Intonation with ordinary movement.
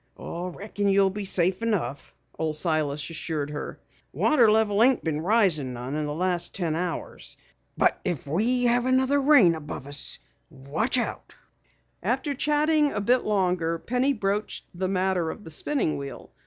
No: wide, 6.7 semitones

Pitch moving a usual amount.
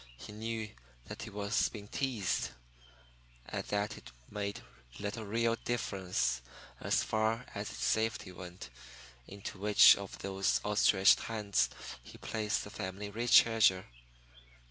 No: narrow, 2.3 semitones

